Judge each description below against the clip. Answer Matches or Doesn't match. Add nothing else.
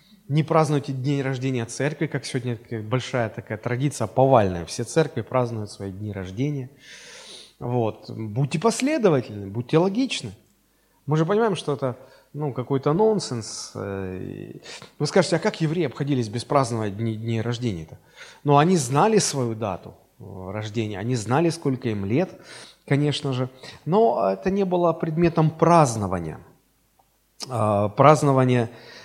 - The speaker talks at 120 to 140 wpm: Matches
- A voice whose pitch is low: Matches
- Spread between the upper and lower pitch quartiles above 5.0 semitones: Matches